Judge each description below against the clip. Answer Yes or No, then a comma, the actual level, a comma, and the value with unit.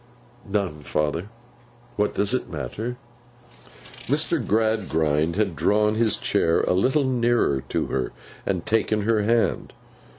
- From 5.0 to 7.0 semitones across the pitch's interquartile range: Yes, wide, 5.4 semitones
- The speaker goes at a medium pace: No, slow, 125 wpm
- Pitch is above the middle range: No, low, 105 Hz